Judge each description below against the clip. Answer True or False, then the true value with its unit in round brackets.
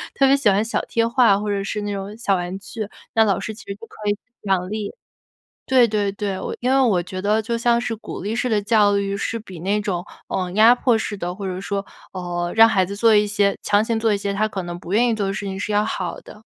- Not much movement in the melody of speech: True (2.3 semitones)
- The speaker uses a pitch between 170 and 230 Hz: True (205 Hz)